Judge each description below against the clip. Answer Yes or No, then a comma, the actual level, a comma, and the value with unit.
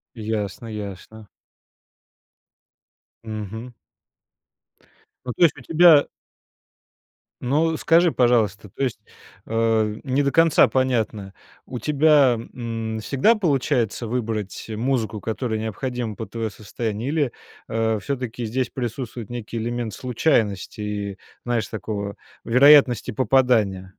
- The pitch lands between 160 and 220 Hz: No, low, 115 Hz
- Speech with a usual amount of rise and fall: Yes, average, 3.4 semitones